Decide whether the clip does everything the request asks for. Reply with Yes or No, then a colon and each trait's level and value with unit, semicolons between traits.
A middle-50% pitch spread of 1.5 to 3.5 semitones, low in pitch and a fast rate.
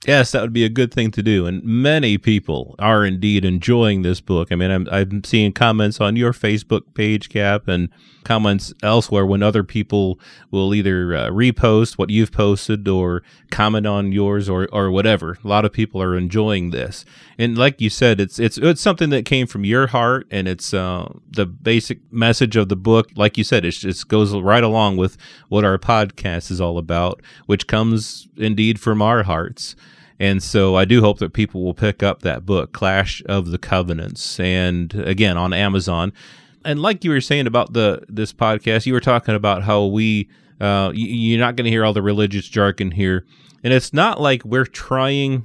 No: average, 3.2 semitones; low, 105 Hz; average, 195 wpm